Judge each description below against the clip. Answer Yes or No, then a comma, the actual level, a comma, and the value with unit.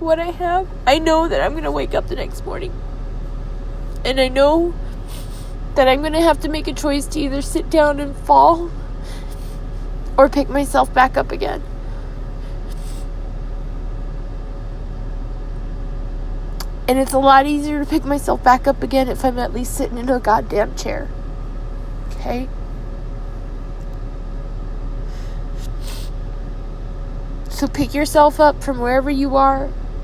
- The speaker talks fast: No, slow, 135 wpm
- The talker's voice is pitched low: No, very high, 285 Hz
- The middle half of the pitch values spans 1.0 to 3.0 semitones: Yes, narrow, 2.5 semitones